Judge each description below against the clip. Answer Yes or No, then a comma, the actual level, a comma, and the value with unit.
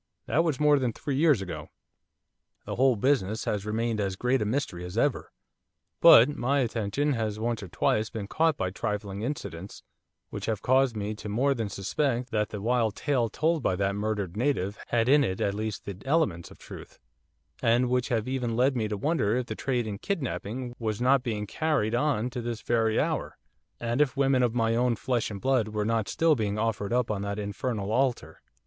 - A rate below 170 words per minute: No, fast, 205 wpm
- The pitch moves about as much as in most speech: Yes, average, 4.0 semitones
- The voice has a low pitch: Yes, low, 115 Hz